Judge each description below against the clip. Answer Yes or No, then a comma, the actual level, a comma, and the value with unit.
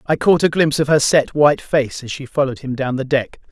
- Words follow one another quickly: Yes, fast, 275 wpm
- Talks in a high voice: No, medium, 140 Hz